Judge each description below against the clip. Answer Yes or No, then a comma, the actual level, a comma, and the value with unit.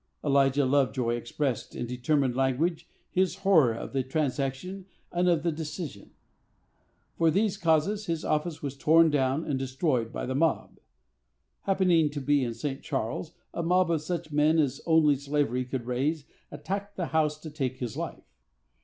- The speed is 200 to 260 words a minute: No, average, 160 wpm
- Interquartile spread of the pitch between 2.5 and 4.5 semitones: Yes, average, 3.9 semitones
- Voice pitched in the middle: Yes, medium, 150 Hz